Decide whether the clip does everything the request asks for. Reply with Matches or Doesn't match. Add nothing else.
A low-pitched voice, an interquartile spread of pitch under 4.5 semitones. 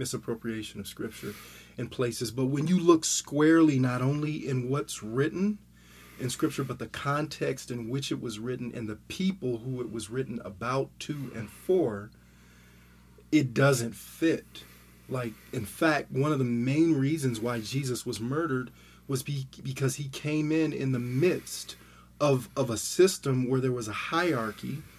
Matches